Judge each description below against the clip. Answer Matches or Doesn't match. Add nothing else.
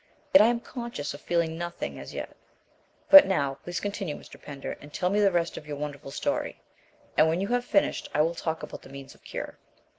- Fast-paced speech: Matches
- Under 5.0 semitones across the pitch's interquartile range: Doesn't match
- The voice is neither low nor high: Matches